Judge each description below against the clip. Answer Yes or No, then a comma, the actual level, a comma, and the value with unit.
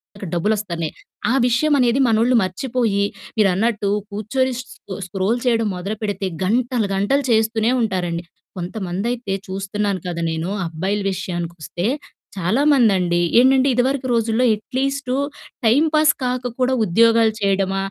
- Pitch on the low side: No, high, 215 Hz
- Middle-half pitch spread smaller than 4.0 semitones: No, average, 4.5 semitones